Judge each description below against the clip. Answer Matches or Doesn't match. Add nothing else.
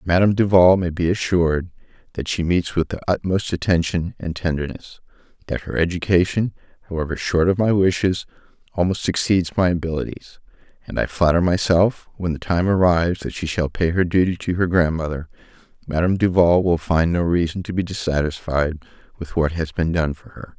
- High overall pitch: Doesn't match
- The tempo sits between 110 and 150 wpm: Doesn't match